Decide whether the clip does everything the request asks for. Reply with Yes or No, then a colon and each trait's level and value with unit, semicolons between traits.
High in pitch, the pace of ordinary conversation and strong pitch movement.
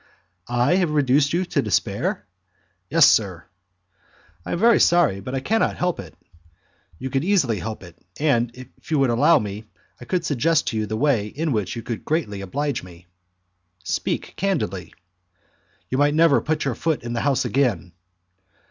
No: low, 135 Hz; average, 175 wpm; wide, 6.4 semitones